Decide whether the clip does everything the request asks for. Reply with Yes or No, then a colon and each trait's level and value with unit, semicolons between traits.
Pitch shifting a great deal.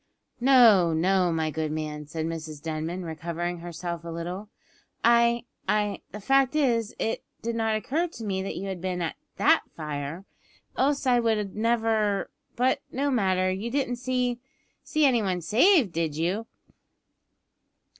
Yes: wide, 5.9 semitones